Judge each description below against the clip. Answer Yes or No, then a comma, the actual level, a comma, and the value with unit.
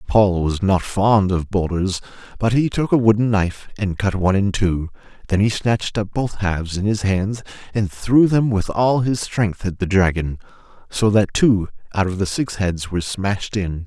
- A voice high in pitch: No, low, 100 Hz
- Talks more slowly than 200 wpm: No, fast, 205 wpm